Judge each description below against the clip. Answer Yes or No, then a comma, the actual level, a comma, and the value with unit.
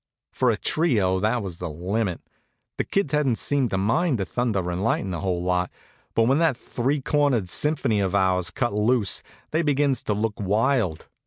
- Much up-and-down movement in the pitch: Yes, wide, 6.2 semitones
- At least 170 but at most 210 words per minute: Yes, average, 185 wpm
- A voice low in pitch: Yes, low, 110 Hz